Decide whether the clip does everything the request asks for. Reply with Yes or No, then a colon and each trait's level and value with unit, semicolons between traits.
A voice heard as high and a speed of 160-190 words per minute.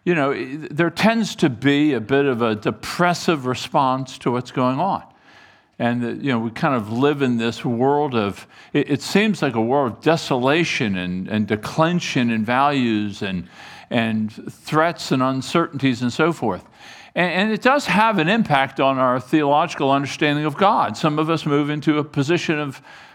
No: medium, 140 Hz; average, 175 wpm